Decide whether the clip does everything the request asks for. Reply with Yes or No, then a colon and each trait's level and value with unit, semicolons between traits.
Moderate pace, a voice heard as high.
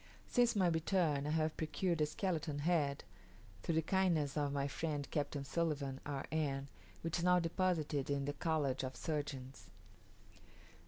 No: average, 155 wpm; medium, 150 Hz